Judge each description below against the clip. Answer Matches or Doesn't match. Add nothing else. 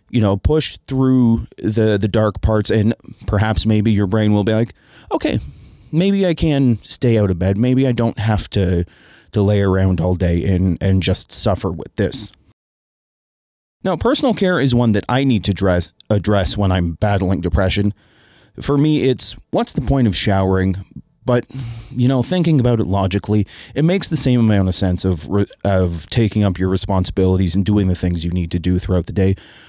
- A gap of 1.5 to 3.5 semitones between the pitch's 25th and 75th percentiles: Doesn't match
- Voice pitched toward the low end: Matches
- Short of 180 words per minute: Doesn't match